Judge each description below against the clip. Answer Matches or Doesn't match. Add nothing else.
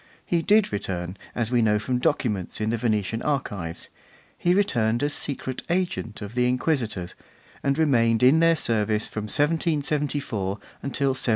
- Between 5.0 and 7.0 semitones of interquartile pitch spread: Matches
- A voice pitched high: Doesn't match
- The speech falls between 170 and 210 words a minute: Doesn't match